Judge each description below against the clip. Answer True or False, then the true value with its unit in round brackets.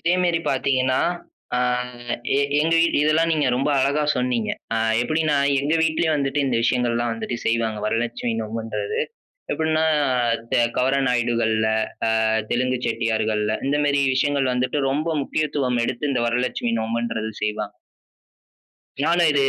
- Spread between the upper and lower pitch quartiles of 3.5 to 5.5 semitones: True (4.1 semitones)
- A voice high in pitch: False (125 Hz)